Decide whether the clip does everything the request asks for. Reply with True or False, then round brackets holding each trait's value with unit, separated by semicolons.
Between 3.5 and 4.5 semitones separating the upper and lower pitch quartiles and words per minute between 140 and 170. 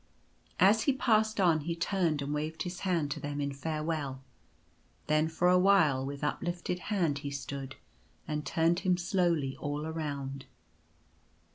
True (3.8 semitones; 150 wpm)